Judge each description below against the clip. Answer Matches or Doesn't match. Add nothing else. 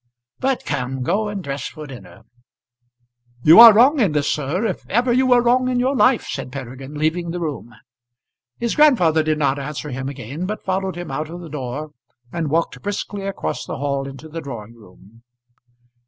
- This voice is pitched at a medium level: Matches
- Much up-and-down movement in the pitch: Matches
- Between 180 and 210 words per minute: Matches